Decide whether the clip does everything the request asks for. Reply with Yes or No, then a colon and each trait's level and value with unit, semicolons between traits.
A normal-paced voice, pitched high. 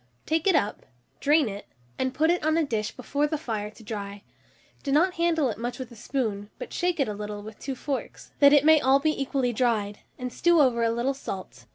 No: fast, 235 wpm; very high, 260 Hz